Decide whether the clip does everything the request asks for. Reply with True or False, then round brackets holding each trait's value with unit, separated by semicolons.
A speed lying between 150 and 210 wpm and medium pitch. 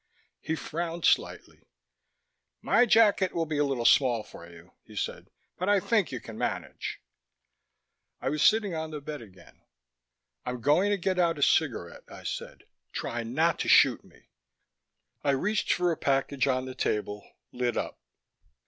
True (165 wpm; 150 Hz)